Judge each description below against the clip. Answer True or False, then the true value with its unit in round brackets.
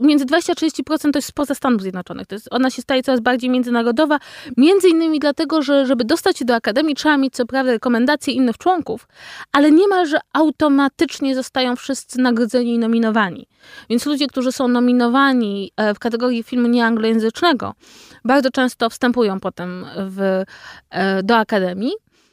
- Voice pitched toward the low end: False (255 Hz)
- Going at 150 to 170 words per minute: True (155 wpm)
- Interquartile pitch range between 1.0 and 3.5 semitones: False (4.0 semitones)